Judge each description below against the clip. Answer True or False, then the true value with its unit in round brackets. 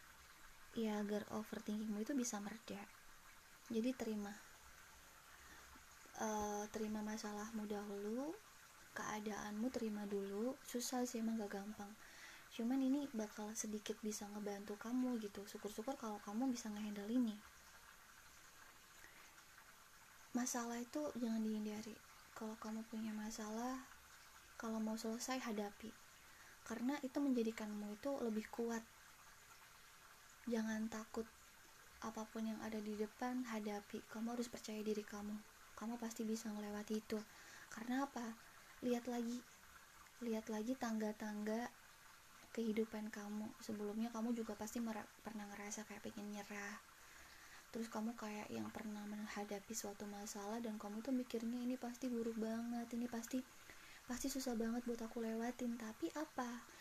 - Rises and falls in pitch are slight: True (2.0 semitones)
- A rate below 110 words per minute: False (120 wpm)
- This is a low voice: False (220 Hz)